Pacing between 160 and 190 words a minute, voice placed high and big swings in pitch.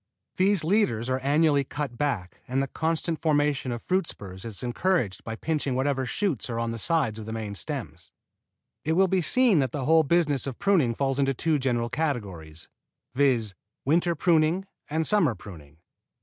No: average, 175 wpm; medium, 140 Hz; wide, 5.7 semitones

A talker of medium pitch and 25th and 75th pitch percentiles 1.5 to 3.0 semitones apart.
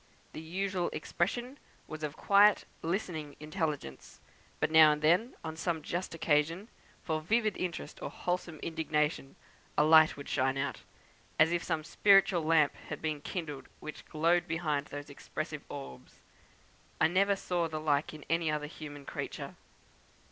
Yes: medium, 160 Hz; narrow, 2.6 semitones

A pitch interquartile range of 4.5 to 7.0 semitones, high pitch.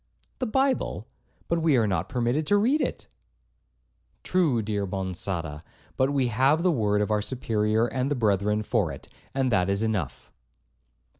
No: wide, 5.6 semitones; low, 115 Hz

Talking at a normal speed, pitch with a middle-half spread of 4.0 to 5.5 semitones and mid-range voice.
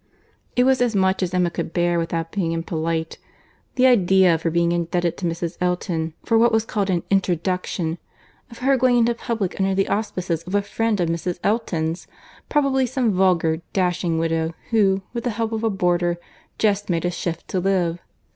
Yes: average, 185 wpm; average, 4.3 semitones; medium, 180 Hz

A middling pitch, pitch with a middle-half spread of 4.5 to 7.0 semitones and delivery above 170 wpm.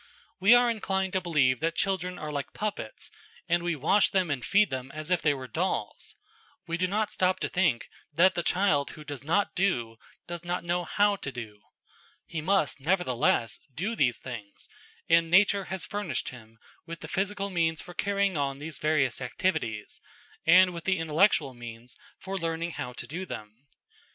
Yes: medium, 165 Hz; wide, 5.5 semitones; average, 180 wpm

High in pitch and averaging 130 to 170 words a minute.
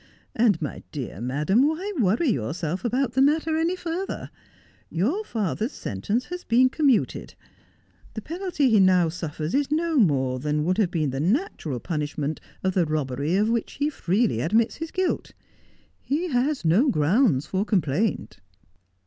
Yes: high, 210 Hz; average, 155 wpm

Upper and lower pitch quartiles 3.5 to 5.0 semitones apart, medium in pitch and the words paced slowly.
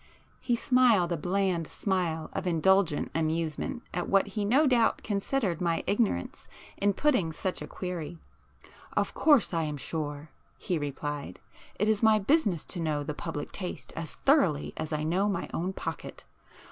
No: average, 4.7 semitones; medium, 180 Hz; average, 160 wpm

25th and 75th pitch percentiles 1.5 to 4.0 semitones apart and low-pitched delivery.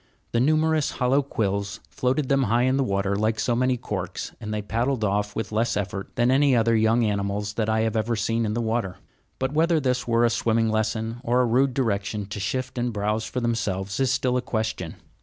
Yes: average, 3.2 semitones; low, 115 Hz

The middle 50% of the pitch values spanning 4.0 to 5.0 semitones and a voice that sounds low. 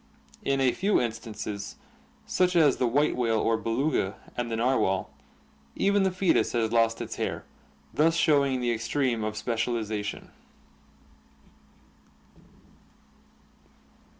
Yes: average, 4.3 semitones; low, 120 Hz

